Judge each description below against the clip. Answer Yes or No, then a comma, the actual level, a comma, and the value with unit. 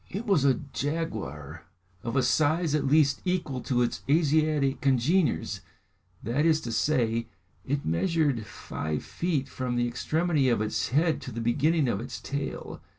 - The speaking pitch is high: No, medium, 140 Hz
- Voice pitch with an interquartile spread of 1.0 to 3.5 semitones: No, average, 4.8 semitones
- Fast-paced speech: No, average, 155 wpm